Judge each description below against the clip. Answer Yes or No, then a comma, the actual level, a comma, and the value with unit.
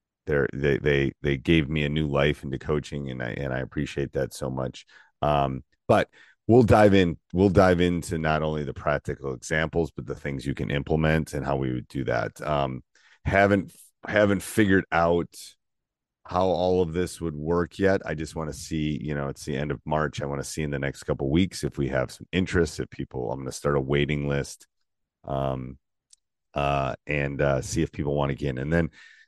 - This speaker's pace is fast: Yes, fast, 215 wpm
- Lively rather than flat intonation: No, average, 3.2 semitones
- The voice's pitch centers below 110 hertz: Yes, very low, 75 Hz